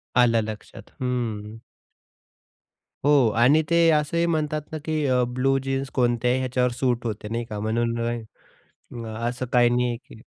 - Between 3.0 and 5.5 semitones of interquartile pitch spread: No, narrow, 2.6 semitones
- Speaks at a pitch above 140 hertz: No, low, 125 Hz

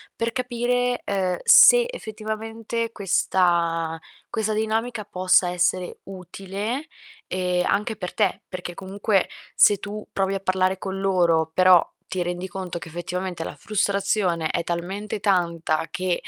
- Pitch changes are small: No, average, 3.2 semitones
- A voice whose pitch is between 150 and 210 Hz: Yes, high, 190 Hz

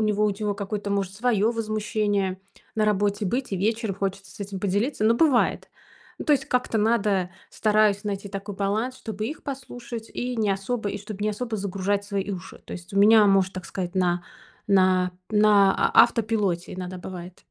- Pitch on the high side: Yes, high, 205 Hz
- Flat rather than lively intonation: Yes, narrow, 2.1 semitones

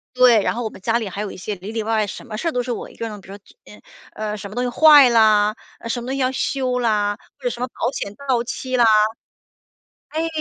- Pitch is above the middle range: Yes, high, 230 Hz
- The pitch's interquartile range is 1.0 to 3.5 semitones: Yes, average, 3.1 semitones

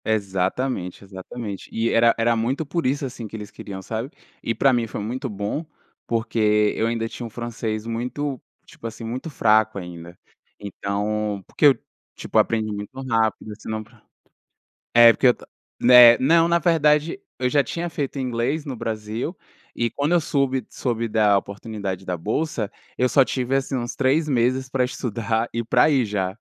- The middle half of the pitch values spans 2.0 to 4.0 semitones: Yes, average, 3.6 semitones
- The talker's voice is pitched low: Yes, low, 115 Hz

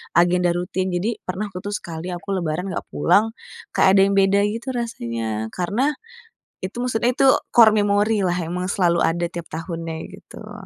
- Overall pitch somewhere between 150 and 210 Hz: Yes, medium, 185 Hz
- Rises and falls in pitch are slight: No, average, 3.2 semitones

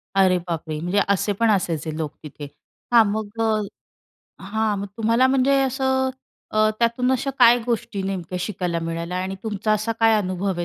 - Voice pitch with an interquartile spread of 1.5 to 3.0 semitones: No, average, 4.1 semitones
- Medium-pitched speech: No, high, 210 Hz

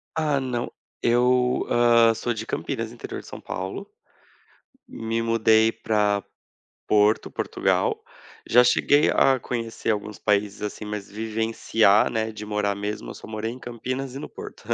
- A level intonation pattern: Yes, narrow, 2.3 semitones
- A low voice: Yes, low, 115 Hz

